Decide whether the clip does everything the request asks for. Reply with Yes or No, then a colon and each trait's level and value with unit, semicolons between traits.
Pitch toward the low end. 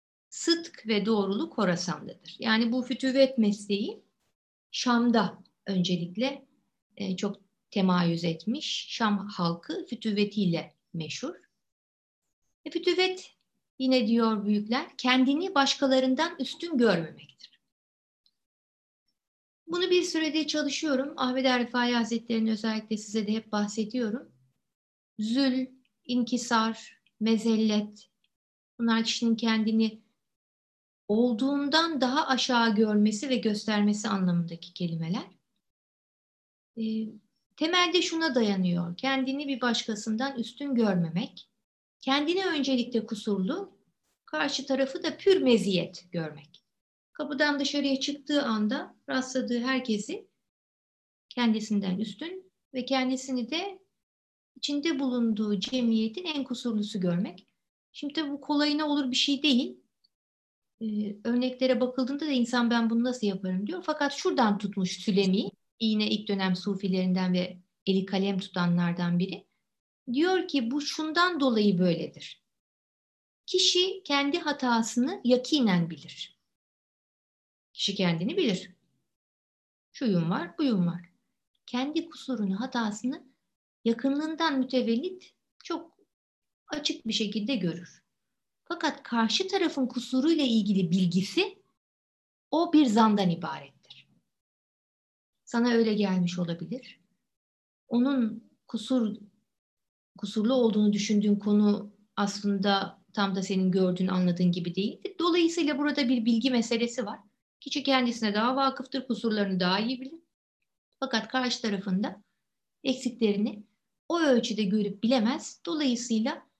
No: high, 230 Hz